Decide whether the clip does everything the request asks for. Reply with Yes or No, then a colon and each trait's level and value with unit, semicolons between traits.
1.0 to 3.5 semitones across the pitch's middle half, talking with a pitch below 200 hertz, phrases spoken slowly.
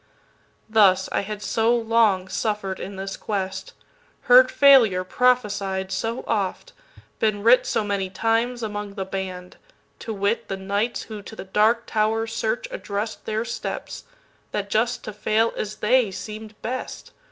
No: average, 2.9 semitones; high, 215 Hz; slow, 130 wpm